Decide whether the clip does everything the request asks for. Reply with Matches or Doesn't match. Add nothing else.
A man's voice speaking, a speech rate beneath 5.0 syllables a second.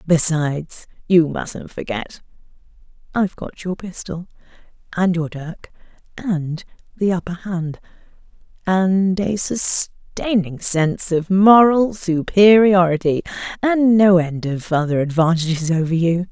Doesn't match